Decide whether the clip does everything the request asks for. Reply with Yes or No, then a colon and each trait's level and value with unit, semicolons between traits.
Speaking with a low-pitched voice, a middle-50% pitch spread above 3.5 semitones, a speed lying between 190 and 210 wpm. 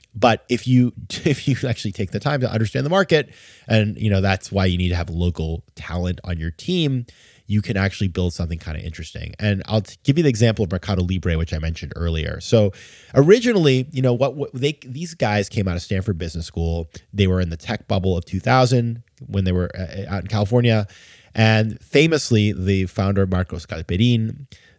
Yes: low, 105 Hz; average, 5.1 semitones; average, 200 wpm